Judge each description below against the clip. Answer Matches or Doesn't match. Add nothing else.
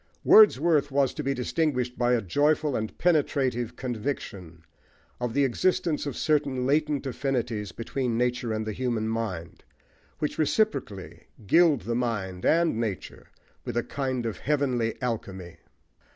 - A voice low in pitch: Matches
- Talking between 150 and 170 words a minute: Doesn't match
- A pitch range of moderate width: Matches